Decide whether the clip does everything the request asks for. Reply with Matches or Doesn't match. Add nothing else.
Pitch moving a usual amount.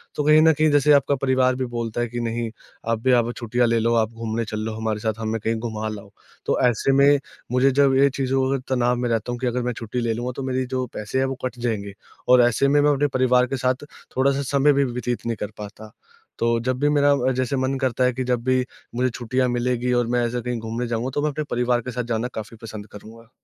Doesn't match